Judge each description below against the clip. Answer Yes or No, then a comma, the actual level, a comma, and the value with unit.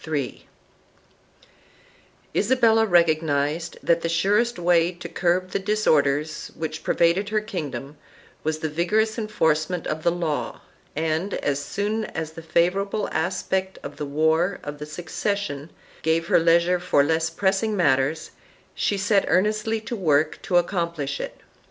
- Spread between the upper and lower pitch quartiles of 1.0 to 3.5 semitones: No, average, 4.0 semitones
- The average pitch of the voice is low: No, medium, 170 Hz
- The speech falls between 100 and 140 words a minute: Yes, slow, 135 wpm